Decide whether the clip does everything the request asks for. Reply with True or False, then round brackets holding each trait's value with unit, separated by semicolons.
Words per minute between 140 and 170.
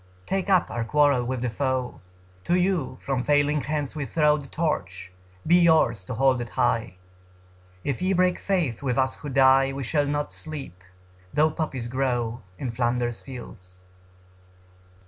True (160 wpm)